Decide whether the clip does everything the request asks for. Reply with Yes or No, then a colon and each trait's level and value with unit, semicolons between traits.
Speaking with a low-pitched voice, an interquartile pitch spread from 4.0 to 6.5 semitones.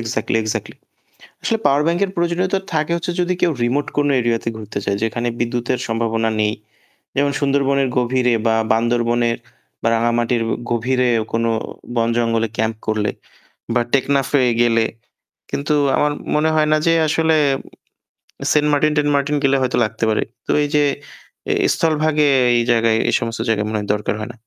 Yes: low, 125 Hz; average, 4.4 semitones